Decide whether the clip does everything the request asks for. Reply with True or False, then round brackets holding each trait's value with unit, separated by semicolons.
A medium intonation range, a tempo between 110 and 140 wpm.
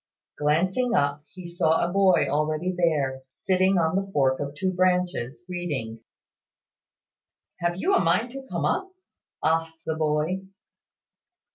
True (3.7 semitones; 135 wpm)